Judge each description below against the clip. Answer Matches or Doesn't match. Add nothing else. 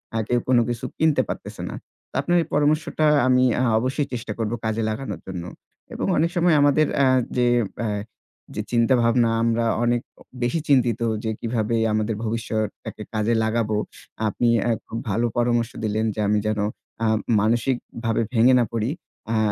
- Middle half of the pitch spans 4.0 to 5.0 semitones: Doesn't match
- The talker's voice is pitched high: Doesn't match